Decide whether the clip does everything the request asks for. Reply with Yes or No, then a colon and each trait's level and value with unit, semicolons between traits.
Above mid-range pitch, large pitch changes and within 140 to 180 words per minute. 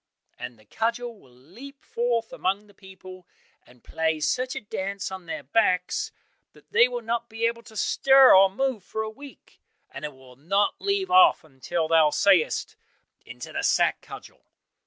Yes: high, 200 Hz; wide, 6.6 semitones; average, 175 wpm